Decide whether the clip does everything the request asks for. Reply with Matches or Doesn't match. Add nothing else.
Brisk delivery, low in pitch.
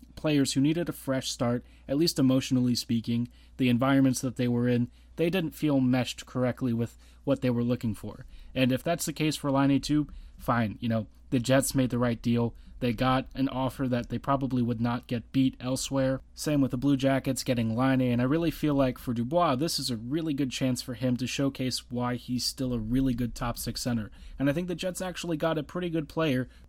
Matches